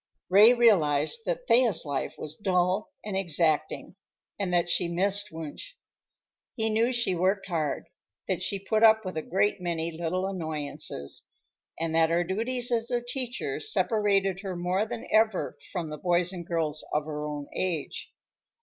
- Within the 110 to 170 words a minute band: Yes, average, 160 wpm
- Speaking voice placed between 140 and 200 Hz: Yes, medium, 185 Hz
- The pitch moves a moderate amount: Yes, average, 4.9 semitones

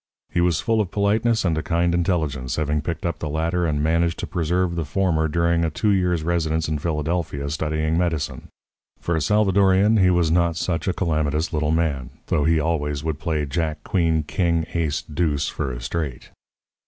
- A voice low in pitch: Yes, very low, 80 Hz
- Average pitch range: No, narrow, 2.3 semitones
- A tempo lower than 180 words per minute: No, average, 190 wpm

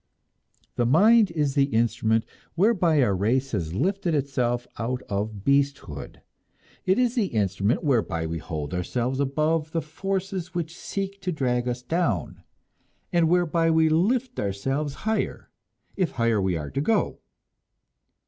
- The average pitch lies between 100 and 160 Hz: Yes, medium, 140 Hz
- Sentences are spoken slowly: No, average, 145 wpm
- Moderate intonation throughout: No, wide, 7.5 semitones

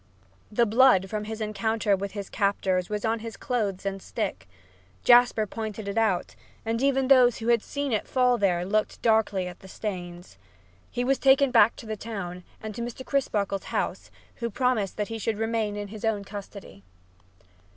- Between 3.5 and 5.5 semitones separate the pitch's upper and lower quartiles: No, average, 2.9 semitones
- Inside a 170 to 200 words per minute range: Yes, average, 180 wpm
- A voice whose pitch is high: Yes, high, 215 Hz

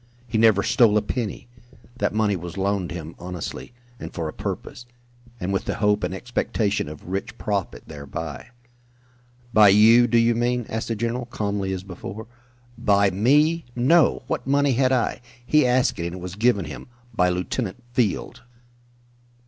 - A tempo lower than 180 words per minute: Yes, average, 165 wpm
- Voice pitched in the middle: No, low, 105 Hz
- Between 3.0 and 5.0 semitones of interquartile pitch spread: Yes, average, 4.4 semitones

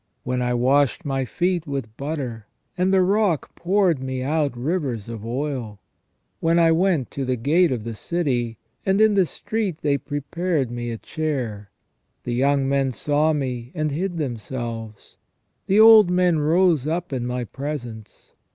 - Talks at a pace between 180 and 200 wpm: No, average, 160 wpm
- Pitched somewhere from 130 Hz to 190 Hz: Yes, medium, 140 Hz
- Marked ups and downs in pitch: Yes, wide, 5.7 semitones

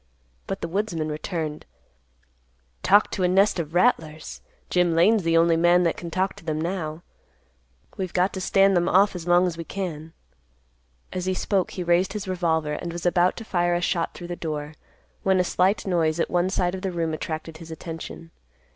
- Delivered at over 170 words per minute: Yes, average, 200 wpm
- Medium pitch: Yes, medium, 175 Hz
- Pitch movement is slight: Yes, narrow, 2.2 semitones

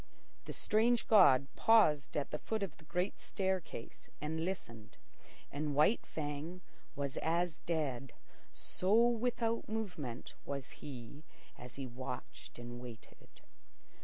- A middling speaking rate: No, slow, 125 wpm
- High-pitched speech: No, medium, 155 Hz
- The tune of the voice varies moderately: No, wide, 6.2 semitones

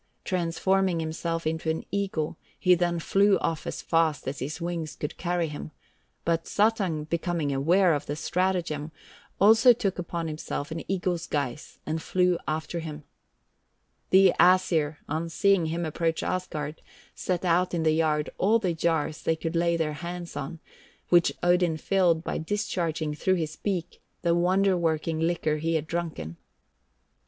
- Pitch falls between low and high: Yes, medium, 170 Hz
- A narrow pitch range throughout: Yes, narrow, 2.3 semitones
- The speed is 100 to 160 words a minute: Yes, average, 155 wpm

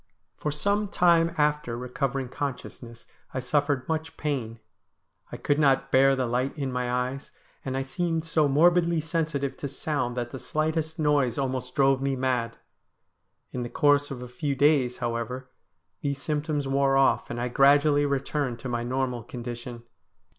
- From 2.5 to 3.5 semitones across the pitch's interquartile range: Yes, average, 3.0 semitones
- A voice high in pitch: No, low, 135 Hz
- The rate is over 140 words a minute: Yes, average, 165 wpm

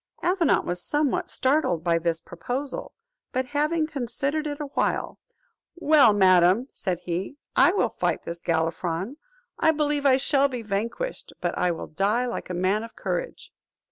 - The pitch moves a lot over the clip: Yes, wide, 8.4 semitones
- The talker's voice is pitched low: No, high, 245 Hz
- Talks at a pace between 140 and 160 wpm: Yes, average, 155 wpm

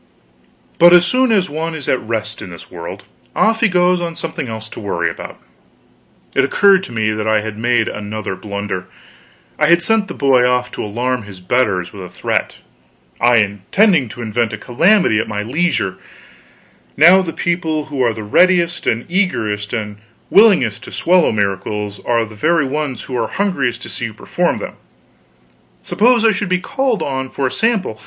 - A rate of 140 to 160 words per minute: No, average, 185 wpm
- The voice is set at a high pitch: No, low, 125 Hz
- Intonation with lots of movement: Yes, wide, 8.4 semitones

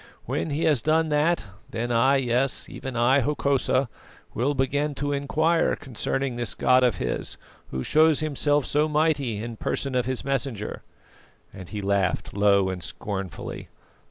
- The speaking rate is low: No, average, 155 wpm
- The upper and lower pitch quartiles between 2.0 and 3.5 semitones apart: No, average, 4.1 semitones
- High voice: No, low, 135 Hz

